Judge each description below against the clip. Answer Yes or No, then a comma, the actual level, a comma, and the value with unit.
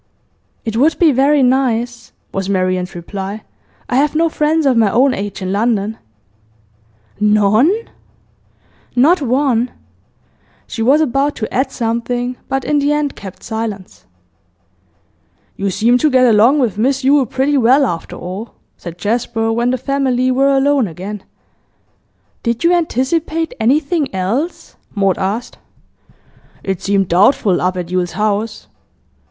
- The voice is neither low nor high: No, high, 240 Hz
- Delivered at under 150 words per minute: Yes, slow, 135 wpm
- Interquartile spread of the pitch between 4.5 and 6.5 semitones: Yes, average, 5.2 semitones